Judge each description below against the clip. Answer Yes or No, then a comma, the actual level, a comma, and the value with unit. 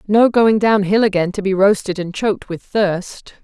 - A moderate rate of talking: No, fast, 210 wpm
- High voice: Yes, high, 200 Hz